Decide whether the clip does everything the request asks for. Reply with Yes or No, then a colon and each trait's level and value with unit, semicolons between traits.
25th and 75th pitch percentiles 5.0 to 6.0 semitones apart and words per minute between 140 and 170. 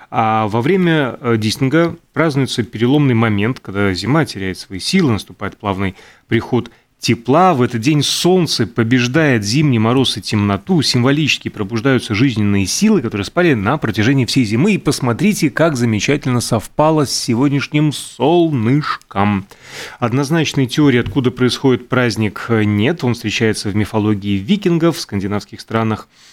No: average, 5.3 semitones; average, 130 wpm